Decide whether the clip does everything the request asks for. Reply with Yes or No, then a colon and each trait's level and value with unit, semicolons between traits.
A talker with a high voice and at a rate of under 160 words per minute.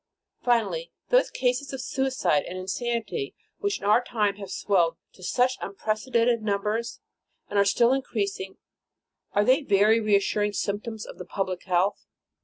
Yes: high, 215 Hz; average, 150 wpm